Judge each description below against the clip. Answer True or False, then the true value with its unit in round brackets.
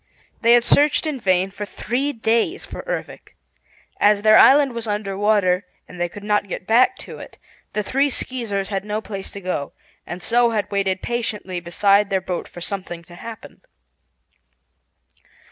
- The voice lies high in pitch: True (205 Hz)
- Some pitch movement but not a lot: True (3.5 semitones)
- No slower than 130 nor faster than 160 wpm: False (170 wpm)